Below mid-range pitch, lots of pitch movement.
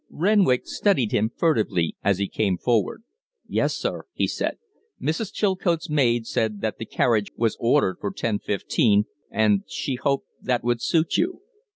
Yes: low, 120 Hz; wide, 6.9 semitones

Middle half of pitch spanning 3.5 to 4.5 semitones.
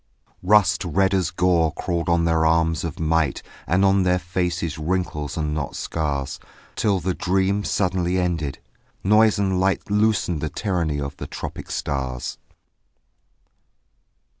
No: average, 3.1 semitones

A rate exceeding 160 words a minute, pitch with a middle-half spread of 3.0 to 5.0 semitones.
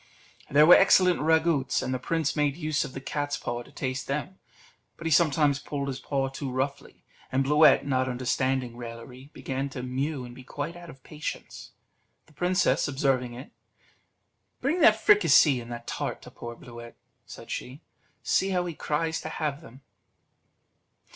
Yes: average, 170 wpm; average, 3.3 semitones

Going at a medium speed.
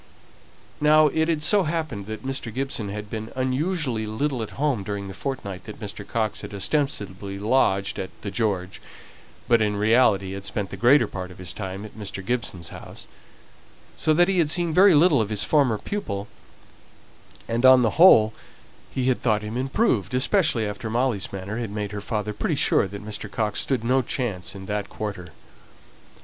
Yes: average, 185 wpm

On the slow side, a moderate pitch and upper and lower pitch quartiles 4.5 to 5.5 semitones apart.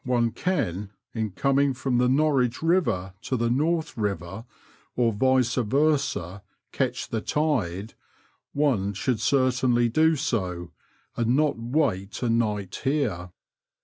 No: slow, 125 wpm; low, 120 Hz; average, 5.1 semitones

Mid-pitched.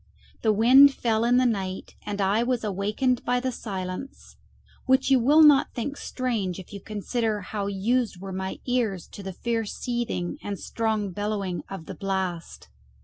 No: high, 215 Hz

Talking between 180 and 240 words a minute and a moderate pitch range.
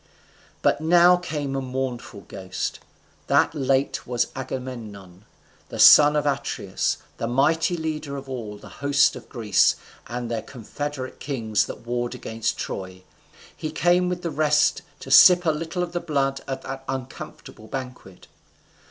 No: average, 145 wpm; average, 4.1 semitones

